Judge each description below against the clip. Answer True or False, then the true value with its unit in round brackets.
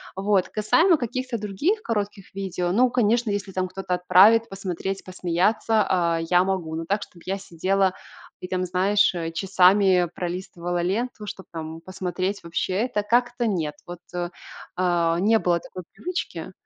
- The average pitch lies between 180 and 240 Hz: True (190 Hz)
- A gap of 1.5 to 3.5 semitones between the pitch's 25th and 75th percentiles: True (2.8 semitones)